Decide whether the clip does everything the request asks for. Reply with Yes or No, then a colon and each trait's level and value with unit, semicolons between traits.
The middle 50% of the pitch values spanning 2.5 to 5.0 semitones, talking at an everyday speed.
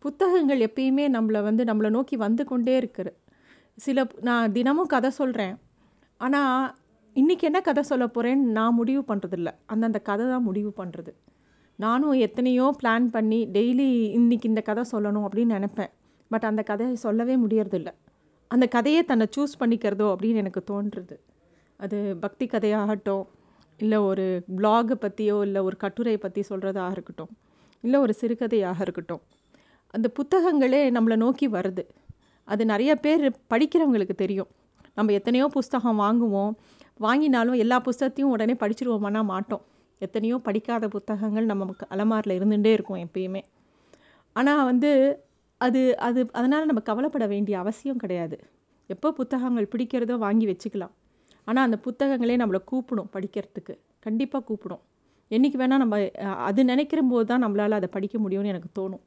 No: average, 3.9 semitones; fast, 135 wpm